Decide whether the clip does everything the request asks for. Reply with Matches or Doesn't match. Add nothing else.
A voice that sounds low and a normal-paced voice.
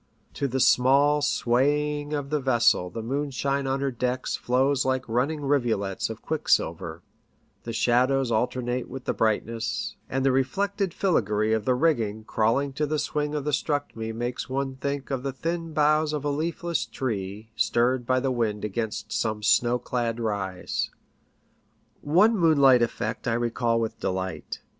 Matches